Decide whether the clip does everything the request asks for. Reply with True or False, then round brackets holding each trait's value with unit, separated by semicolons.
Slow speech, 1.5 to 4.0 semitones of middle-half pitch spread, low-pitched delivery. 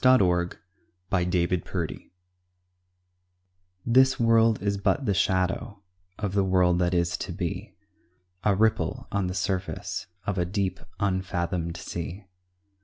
True (120 wpm; 2.5 semitones; 95 Hz)